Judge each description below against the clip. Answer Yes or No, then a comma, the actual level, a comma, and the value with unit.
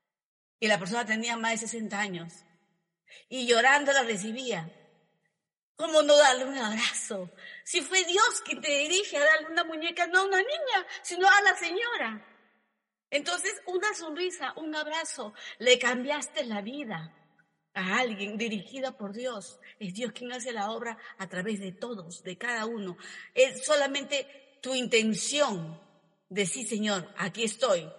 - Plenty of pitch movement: Yes, wide, 6.8 semitones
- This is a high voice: Yes, high, 240 Hz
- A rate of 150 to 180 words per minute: Yes, average, 155 wpm